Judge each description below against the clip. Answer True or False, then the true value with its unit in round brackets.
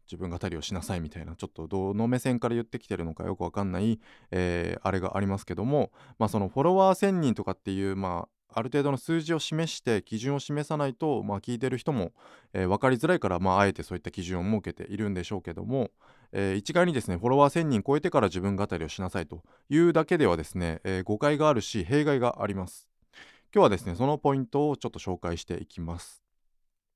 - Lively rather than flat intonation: True (7.0 semitones)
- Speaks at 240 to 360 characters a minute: False (465 characters per minute)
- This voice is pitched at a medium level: False (100 Hz)